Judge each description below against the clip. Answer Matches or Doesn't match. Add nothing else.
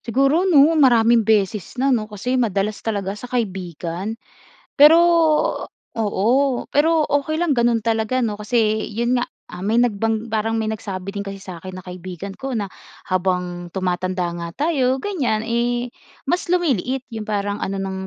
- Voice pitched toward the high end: Matches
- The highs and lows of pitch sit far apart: Doesn't match